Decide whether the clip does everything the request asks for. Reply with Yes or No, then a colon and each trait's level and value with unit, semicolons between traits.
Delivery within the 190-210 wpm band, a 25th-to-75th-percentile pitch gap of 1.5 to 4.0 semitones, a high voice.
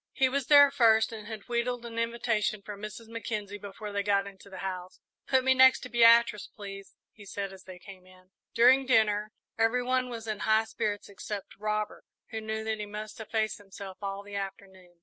Yes: average, 200 wpm; narrow, 2.6 semitones; high, 215 Hz